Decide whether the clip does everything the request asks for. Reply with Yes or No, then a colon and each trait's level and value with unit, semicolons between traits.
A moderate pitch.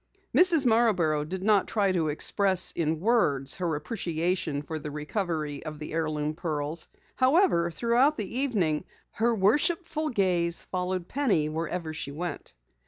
Yes: medium, 175 Hz